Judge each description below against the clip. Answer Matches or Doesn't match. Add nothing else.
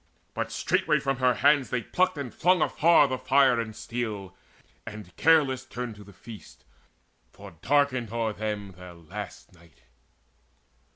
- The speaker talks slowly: Doesn't match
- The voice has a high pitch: Doesn't match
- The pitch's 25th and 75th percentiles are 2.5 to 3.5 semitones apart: Doesn't match